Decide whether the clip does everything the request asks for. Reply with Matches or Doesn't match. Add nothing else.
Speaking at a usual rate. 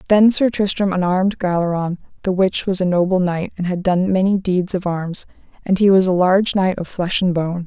Doesn't match